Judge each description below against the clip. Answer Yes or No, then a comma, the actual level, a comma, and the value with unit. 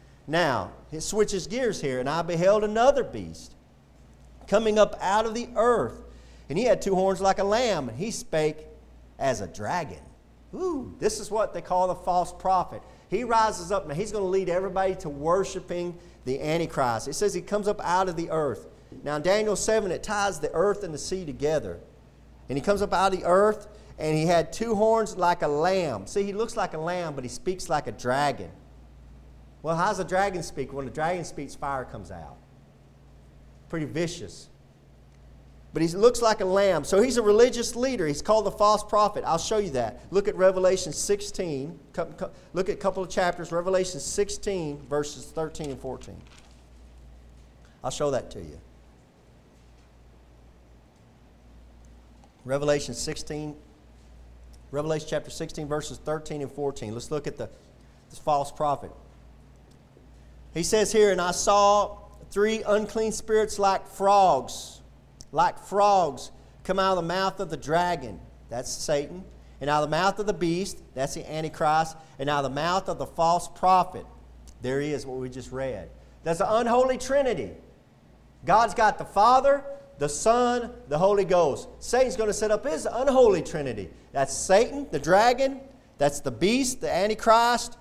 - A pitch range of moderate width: No, wide, 6.9 semitones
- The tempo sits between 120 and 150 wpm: No, average, 175 wpm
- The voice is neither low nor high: Yes, medium, 170 Hz